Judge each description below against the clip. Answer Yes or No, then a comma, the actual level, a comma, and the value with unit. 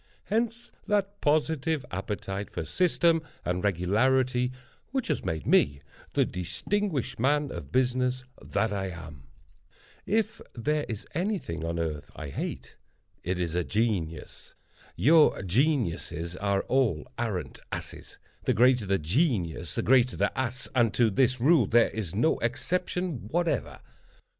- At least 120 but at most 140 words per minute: Yes, slow, 135 wpm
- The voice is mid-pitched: No, low, 120 Hz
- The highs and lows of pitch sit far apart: Yes, wide, 8.8 semitones